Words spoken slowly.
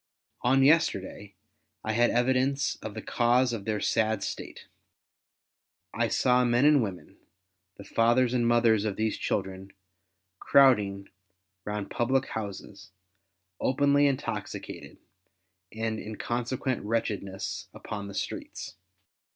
Yes: slow, 115 wpm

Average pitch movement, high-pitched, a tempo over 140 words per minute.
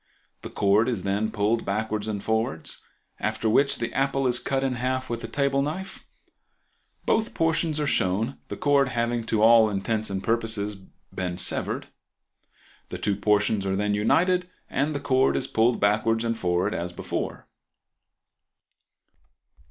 No: average, 4.5 semitones; low, 115 Hz; average, 150 wpm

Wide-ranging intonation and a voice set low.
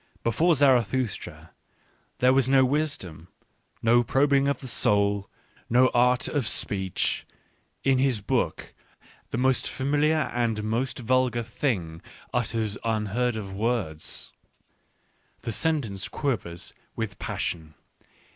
No: average, 4.3 semitones; low, 120 Hz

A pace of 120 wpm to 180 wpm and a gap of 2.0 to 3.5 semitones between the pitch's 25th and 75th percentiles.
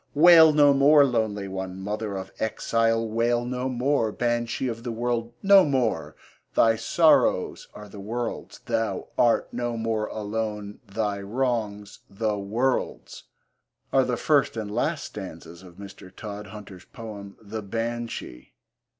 Yes: slow, 135 wpm; average, 3.0 semitones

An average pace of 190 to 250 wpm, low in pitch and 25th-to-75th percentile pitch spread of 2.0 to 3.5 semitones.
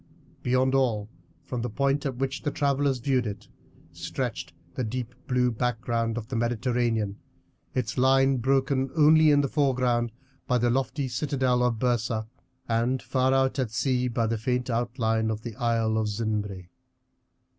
No: average, 155 wpm; low, 125 Hz; narrow, 2.6 semitones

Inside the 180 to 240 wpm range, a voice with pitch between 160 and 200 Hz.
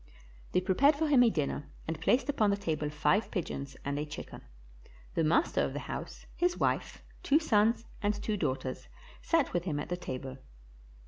Yes: average, 185 wpm; medium, 185 Hz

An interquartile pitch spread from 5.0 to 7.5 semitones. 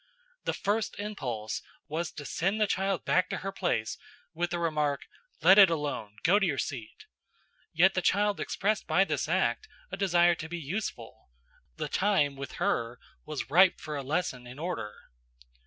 Yes: average, 5.3 semitones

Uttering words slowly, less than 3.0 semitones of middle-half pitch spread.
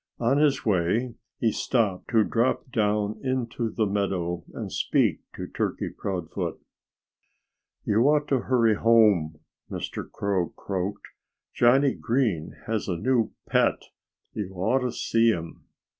No: slow, 130 wpm; average, 4.2 semitones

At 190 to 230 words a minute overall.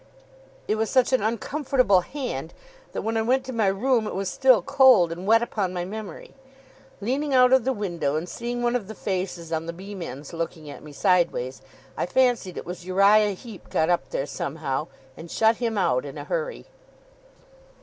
Yes: average, 195 wpm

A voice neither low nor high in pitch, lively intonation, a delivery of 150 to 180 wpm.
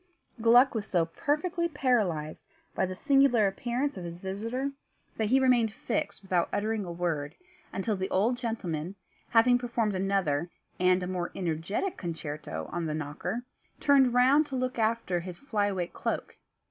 No: high, 205 Hz; wide, 5.9 semitones; average, 160 wpm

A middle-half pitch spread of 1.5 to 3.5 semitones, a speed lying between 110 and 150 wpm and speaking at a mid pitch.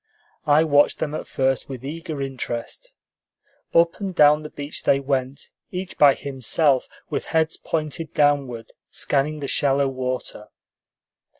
Yes: narrow, 2.5 semitones; slow, 135 wpm; medium, 145 Hz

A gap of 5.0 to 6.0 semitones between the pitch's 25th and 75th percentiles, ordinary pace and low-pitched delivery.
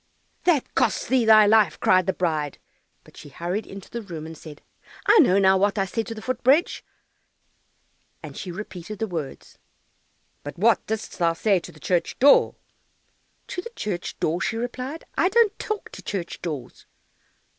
No: wide, 5.6 semitones; average, 175 wpm; high, 200 Hz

